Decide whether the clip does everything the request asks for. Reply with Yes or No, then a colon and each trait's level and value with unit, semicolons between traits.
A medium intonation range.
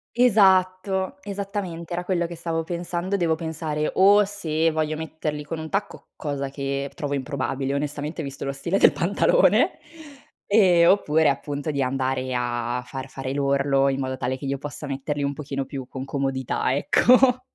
Yes: average, 4.3 semitones